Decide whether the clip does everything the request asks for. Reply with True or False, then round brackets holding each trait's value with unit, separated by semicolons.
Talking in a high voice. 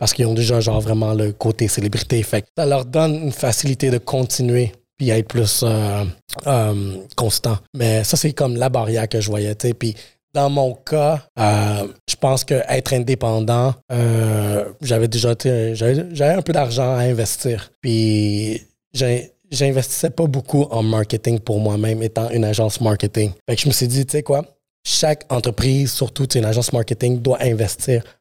False (120 Hz)